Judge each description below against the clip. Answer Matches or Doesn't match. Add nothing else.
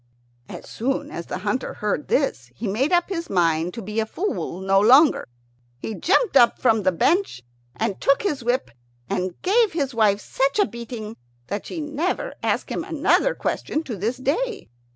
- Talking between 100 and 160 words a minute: Doesn't match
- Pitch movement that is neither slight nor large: Doesn't match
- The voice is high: Matches